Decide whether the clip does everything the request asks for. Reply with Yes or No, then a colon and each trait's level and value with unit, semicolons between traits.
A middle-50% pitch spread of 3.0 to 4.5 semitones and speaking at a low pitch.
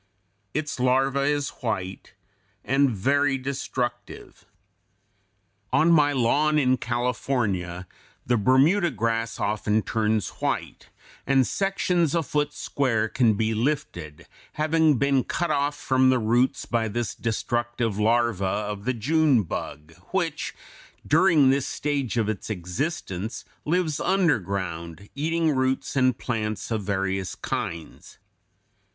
No: average, 5.1 semitones; low, 125 Hz